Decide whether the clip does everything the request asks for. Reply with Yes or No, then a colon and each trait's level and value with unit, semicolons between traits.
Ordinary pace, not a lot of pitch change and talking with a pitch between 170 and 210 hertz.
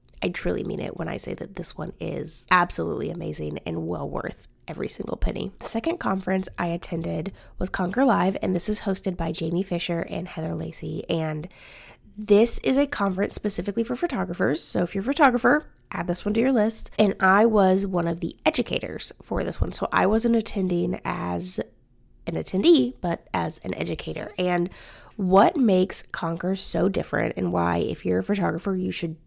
No: average, 185 wpm; average, 4.0 semitones; high, 190 Hz